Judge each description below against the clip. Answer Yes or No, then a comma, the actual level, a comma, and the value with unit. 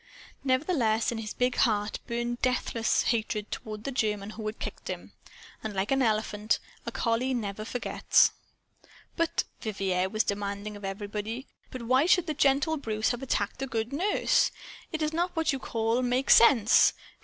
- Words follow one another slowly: No, average, 165 wpm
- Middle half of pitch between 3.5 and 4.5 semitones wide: Yes, average, 3.8 semitones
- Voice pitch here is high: Yes, high, 230 Hz